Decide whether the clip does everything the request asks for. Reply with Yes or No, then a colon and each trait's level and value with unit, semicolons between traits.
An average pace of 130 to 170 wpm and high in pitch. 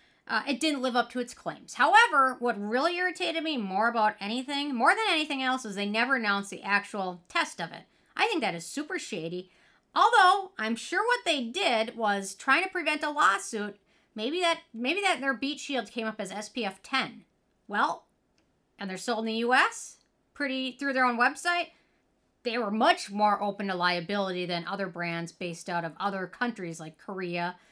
No: average, 195 wpm; high, 235 Hz